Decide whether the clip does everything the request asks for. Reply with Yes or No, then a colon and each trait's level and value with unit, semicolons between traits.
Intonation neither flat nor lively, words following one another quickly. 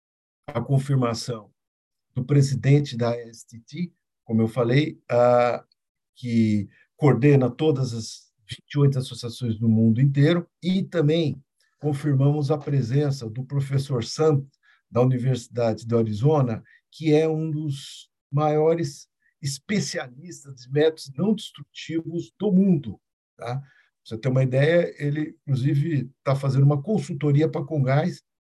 No: average, 4.2 semitones; slow, 120 wpm